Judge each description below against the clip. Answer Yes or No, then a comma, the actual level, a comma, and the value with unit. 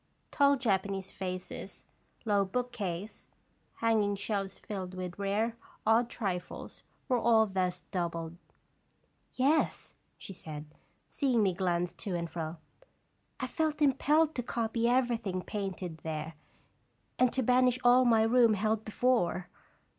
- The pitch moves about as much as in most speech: Yes, average, 5.0 semitones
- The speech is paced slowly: Yes, slow, 130 wpm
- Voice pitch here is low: No, high, 210 Hz